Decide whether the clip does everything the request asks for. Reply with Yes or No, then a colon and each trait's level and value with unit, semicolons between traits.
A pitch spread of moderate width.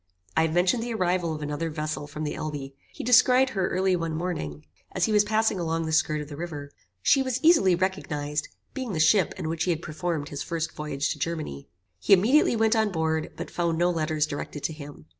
Yes: average, 3.8 semitones